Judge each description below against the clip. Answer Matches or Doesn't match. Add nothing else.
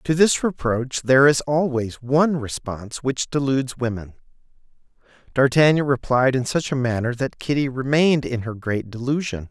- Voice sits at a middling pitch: Doesn't match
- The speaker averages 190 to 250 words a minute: Doesn't match